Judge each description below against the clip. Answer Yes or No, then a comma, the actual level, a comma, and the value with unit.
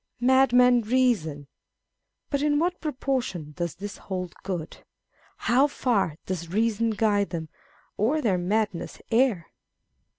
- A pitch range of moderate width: No, wide, 6.0 semitones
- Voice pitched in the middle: No, high, 220 Hz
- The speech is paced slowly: Yes, slow, 125 wpm